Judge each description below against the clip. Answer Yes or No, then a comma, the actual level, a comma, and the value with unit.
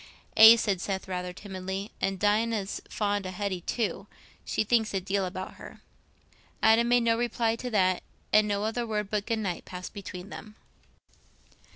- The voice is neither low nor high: No, high, 205 Hz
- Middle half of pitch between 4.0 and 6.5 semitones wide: No, average, 2.8 semitones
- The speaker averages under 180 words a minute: Yes, average, 170 wpm